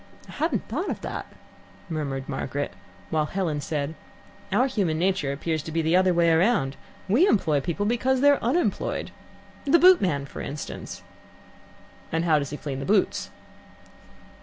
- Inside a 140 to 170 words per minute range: Yes, average, 160 wpm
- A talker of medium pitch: Yes, medium, 165 Hz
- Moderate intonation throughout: No, wide, 7.1 semitones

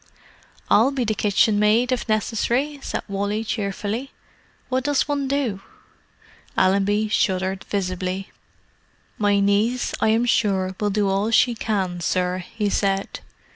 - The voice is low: No, high, 210 Hz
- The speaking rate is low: Yes, slow, 130 wpm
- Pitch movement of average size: Yes, average, 3.0 semitones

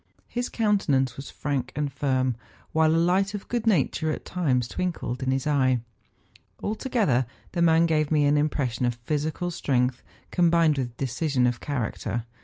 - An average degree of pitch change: Yes, average, 4.6 semitones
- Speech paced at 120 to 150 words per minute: No, average, 165 wpm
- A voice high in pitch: No, medium, 145 Hz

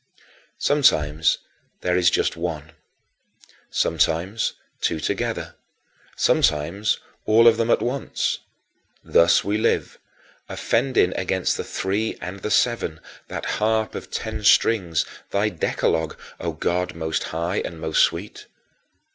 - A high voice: No, very low, 90 Hz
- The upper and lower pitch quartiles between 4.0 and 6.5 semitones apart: Yes, average, 5.0 semitones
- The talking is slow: Yes, slow, 120 wpm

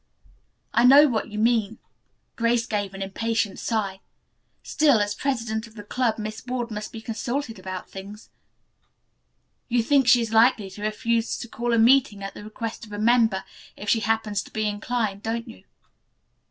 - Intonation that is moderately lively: No, narrow, 2.3 semitones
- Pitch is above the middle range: Yes, high, 225 Hz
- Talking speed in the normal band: Yes, average, 180 wpm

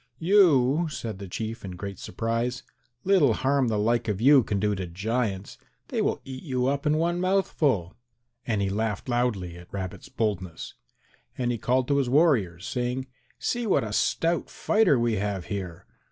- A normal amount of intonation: No, wide, 5.7 semitones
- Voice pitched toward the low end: Yes, low, 120 Hz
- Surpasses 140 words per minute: Yes, average, 175 wpm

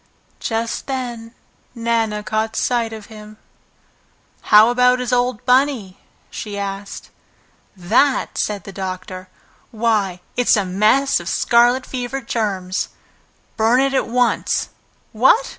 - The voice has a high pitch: Yes, high, 225 Hz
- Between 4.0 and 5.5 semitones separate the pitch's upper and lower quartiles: No, average, 3.4 semitones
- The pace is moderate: No, slow, 120 wpm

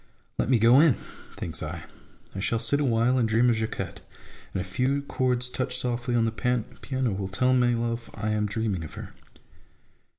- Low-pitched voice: Yes, low, 120 Hz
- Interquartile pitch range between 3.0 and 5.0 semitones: No, narrow, 2.4 semitones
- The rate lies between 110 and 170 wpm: No, average, 190 wpm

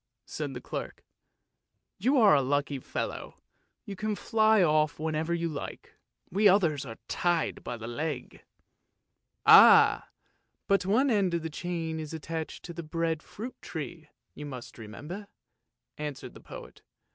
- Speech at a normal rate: Yes, average, 155 wpm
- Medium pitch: Yes, medium, 160 Hz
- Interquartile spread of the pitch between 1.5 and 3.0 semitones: No, average, 4.6 semitones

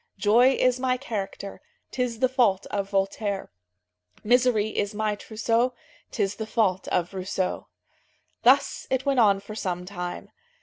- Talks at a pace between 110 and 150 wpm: Yes, average, 140 wpm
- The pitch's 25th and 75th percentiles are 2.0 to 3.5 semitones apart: No, average, 4.0 semitones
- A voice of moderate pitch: No, high, 215 Hz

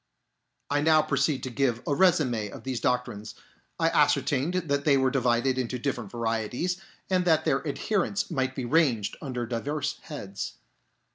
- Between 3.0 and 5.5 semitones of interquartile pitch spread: Yes, average, 4.0 semitones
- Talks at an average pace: Yes, average, 160 wpm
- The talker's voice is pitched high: No, low, 135 Hz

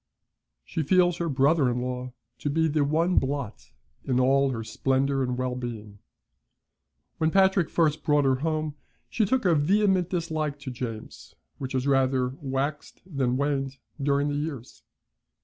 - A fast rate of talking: No, average, 155 wpm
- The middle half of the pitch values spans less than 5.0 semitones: Yes, average, 3.6 semitones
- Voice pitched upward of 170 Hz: No, medium, 140 Hz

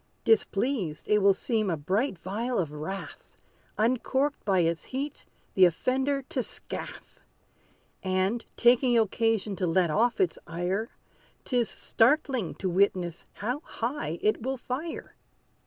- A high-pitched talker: Yes, high, 215 Hz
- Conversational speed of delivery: No, slow, 130 wpm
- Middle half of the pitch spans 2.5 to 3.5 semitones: No, average, 5.3 semitones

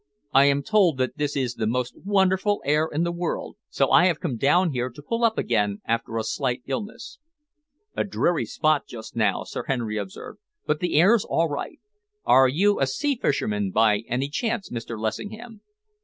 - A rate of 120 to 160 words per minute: No, average, 185 wpm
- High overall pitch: No, medium, 140 Hz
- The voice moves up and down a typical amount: No, wide, 8.0 semitones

